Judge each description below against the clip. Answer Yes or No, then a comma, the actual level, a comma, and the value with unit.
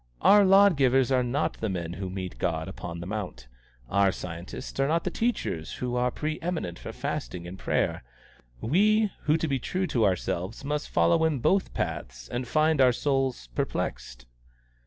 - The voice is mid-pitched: No, low, 125 Hz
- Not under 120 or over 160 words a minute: No, average, 175 wpm